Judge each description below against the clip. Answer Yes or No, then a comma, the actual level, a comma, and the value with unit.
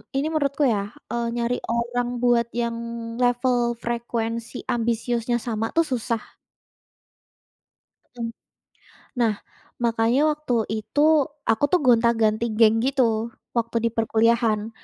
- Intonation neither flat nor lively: No, narrow, 1.4 semitones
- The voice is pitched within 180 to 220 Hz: No, high, 235 Hz